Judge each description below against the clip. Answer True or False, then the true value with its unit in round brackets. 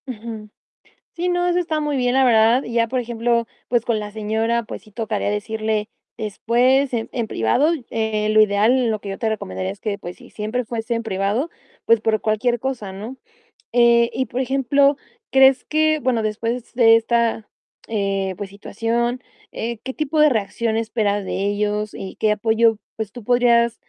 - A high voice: True (230 Hz)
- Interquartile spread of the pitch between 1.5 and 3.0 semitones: True (2.6 semitones)